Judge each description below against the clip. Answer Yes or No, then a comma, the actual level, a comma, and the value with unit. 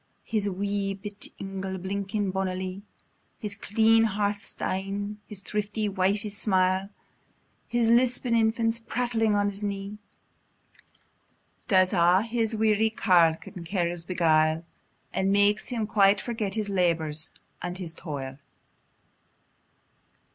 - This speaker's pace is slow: Yes, slow, 115 wpm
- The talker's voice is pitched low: No, high, 200 Hz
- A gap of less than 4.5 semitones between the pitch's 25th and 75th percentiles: Yes, narrow, 2.5 semitones